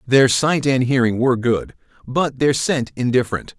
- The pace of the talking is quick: No, average, 165 wpm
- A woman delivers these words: No, male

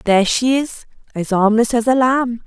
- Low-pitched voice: No, high, 235 Hz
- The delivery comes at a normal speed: Yes, average, 195 wpm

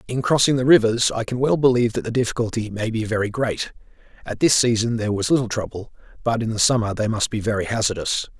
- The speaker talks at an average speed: No, fast, 220 wpm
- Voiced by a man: Yes, male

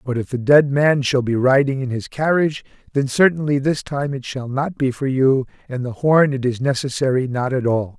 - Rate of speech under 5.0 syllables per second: No, 5.2 syllables/s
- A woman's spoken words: No, male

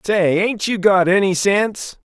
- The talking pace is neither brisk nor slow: Yes, average, 170 wpm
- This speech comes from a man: Yes, male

